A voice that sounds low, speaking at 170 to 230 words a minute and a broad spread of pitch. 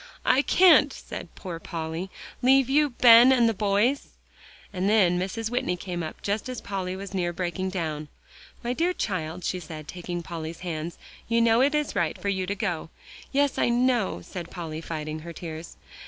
No: high, 190 Hz; average, 185 wpm; wide, 5.8 semitones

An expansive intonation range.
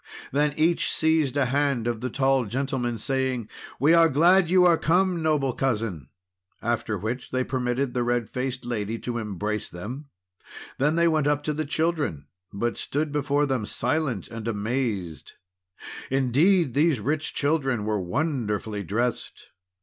No: average, 4.6 semitones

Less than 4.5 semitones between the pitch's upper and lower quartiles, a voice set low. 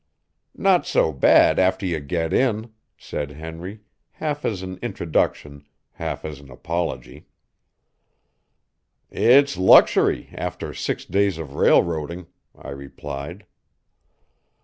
No: average, 5.3 semitones; very low, 85 Hz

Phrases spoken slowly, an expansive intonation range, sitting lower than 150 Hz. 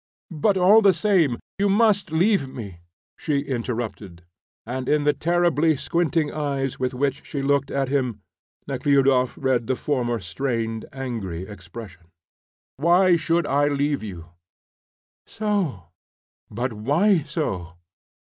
Yes: slow, 125 wpm; wide, 5.8 semitones; medium, 140 Hz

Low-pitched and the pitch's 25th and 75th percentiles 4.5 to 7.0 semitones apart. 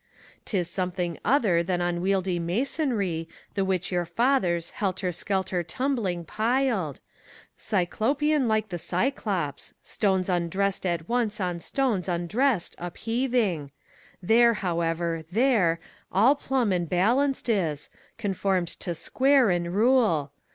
No: high, 190 Hz; average, 5.3 semitones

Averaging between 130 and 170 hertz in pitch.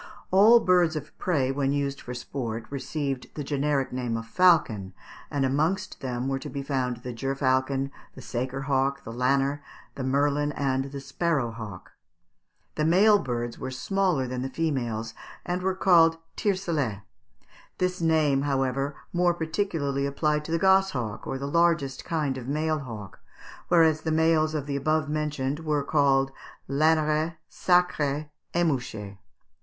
Yes: medium, 140 Hz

